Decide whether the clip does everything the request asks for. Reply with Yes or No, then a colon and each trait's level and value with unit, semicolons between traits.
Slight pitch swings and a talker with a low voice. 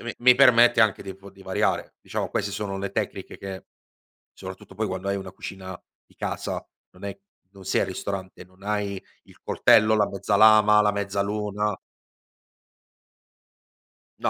Yes: narrow, 1.7 semitones; low, 100 Hz